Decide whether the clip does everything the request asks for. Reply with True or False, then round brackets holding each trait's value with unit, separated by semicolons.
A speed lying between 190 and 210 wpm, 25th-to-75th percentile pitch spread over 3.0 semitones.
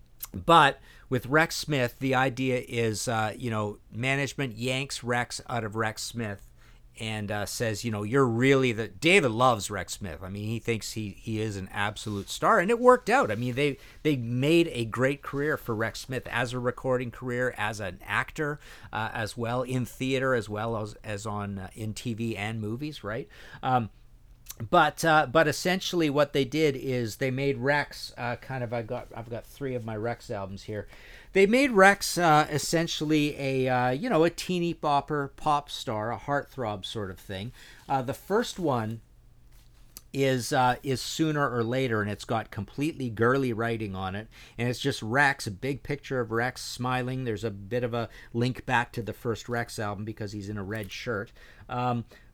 True (195 wpm; 3.9 semitones)